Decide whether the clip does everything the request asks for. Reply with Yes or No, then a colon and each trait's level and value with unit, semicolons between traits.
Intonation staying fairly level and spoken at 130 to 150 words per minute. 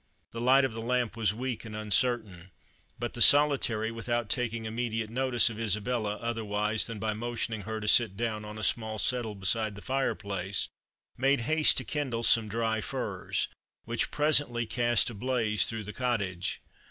No: narrow, 2.3 semitones; average, 170 wpm